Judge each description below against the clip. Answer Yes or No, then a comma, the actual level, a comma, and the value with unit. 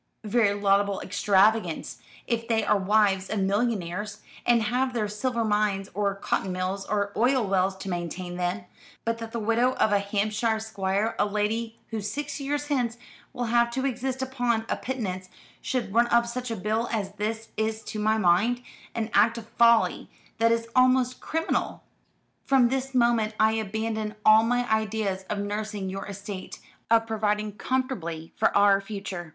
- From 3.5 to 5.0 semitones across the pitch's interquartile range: No, average, 2.8 semitones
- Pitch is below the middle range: No, high, 220 Hz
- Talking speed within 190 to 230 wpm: No, average, 170 wpm